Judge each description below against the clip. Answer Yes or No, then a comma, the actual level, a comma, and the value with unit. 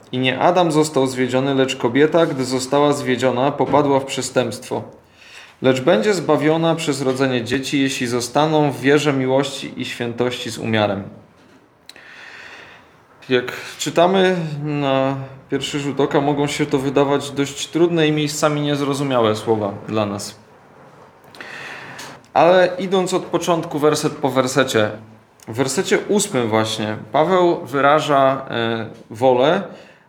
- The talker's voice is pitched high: No, medium, 140 Hz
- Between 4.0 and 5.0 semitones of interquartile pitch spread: No, average, 3.0 semitones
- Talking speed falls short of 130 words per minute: Yes, average, 120 wpm